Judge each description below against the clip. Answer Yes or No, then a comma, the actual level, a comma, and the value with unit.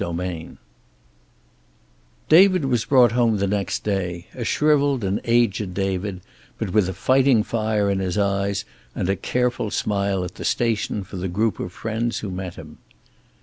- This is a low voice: Yes, low, 100 Hz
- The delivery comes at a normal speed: Yes, average, 160 wpm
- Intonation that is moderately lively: Yes, average, 3.8 semitones